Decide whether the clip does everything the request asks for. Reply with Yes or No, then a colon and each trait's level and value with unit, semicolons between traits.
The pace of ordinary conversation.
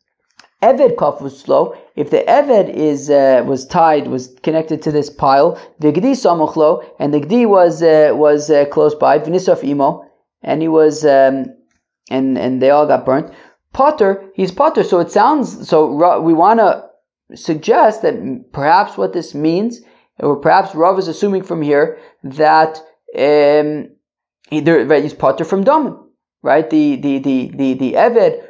Yes: average, 165 wpm